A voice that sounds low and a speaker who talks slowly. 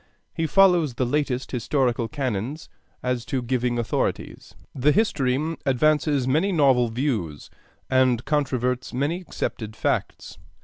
Yes: low, 130 Hz; slow, 120 wpm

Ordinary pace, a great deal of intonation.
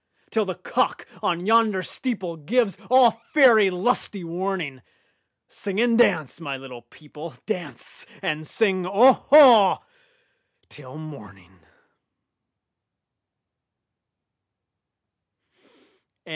No: slow, 75 wpm; wide, 6.9 semitones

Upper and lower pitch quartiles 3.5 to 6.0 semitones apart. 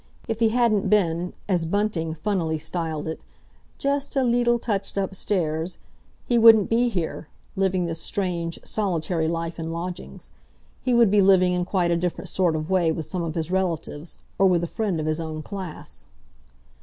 Yes: average, 3.9 semitones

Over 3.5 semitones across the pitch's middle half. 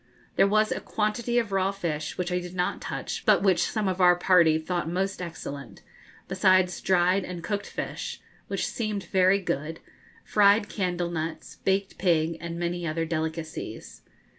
No: average, 2.7 semitones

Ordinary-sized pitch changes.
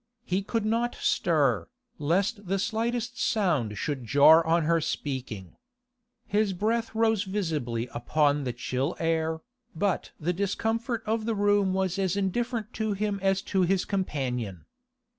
No: wide, 6.1 semitones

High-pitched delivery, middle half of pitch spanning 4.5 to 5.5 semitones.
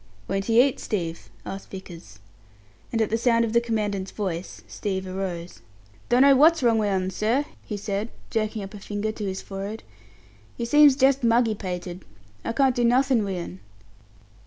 No: high, 215 Hz; average, 3.7 semitones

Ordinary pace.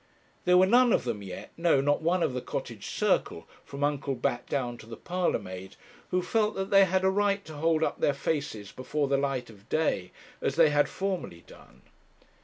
No: fast, 210 wpm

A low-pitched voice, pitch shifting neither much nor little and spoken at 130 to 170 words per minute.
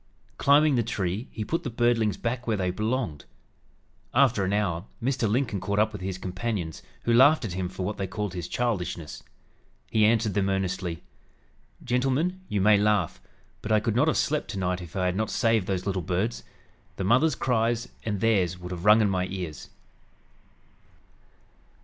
No: low, 105 Hz; average, 4.1 semitones; average, 180 wpm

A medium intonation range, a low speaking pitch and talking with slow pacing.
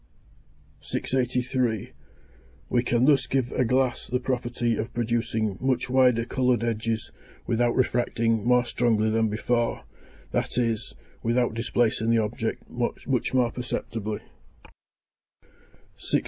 No: narrow, 1.7 semitones; low, 120 Hz; slow, 115 wpm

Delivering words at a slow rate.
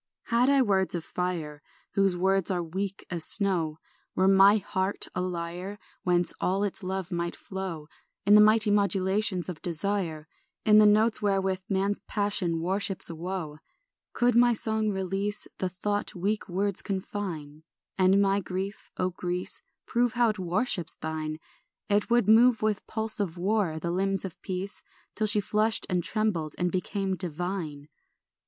No: average, 160 wpm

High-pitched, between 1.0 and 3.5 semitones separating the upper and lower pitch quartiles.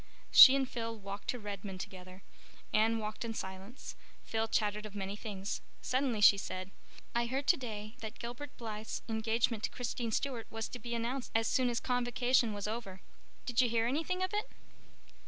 Yes: high, 225 Hz; average, 2.9 semitones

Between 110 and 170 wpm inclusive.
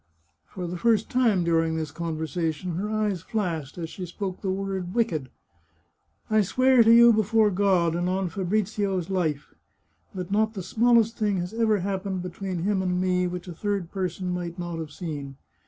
No: average, 180 wpm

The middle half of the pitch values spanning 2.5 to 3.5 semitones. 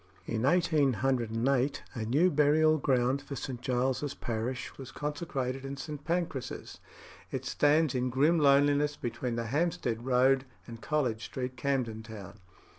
Yes: average, 3.2 semitones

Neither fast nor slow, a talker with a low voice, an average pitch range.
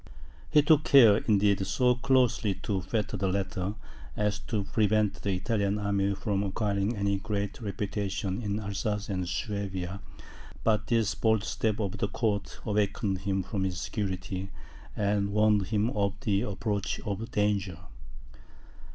No: average, 145 wpm; low, 100 Hz; narrow, 1.6 semitones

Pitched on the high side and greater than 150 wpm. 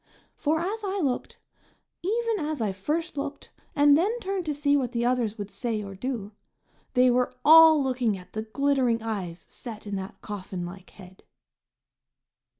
Yes: very high, 250 Hz; average, 165 wpm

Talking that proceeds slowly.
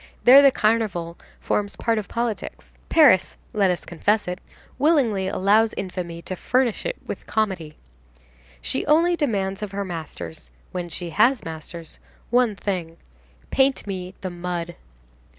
Yes: slow, 125 wpm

